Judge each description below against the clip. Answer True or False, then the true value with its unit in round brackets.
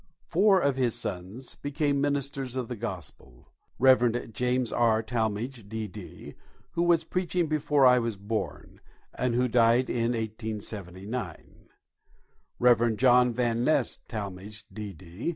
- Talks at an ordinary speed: False (125 wpm)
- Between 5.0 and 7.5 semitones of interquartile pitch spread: False (3.4 semitones)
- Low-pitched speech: True (120 Hz)